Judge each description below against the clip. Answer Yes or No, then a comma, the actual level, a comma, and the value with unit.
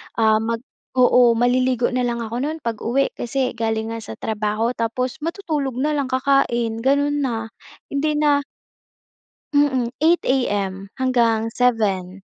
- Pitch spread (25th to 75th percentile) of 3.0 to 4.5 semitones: Yes, average, 3.5 semitones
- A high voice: Yes, high, 245 Hz